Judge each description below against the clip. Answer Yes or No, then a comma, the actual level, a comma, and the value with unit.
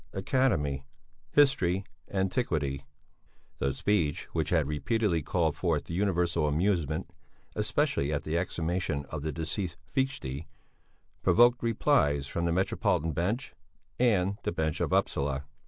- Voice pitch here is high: No, very low, 85 Hz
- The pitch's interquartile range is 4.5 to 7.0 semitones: Yes, average, 5.1 semitones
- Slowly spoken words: Yes, slow, 120 wpm